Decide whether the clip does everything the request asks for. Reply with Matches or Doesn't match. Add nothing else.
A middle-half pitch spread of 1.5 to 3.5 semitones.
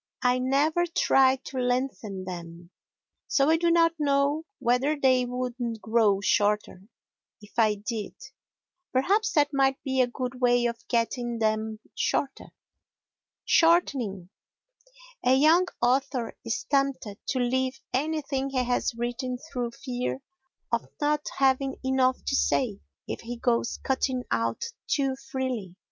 Matches